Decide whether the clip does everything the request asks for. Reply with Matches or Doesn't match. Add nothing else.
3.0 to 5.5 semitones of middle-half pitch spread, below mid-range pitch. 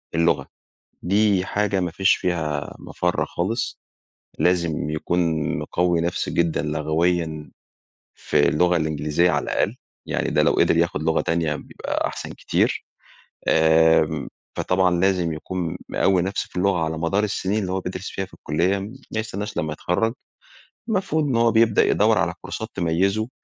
Matches